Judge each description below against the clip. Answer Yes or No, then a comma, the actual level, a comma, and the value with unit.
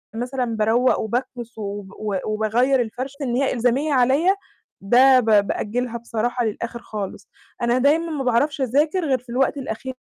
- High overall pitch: Yes, high, 245 Hz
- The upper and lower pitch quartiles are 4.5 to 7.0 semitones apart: No, average, 3.2 semitones